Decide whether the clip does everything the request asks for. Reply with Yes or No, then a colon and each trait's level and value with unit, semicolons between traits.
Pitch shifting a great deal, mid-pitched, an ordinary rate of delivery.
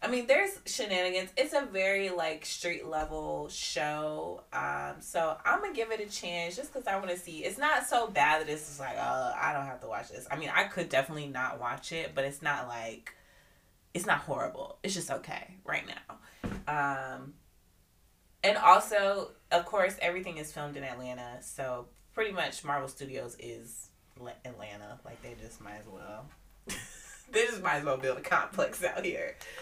Yes: wide, 6.7 semitones; medium, 150 Hz; average, 190 wpm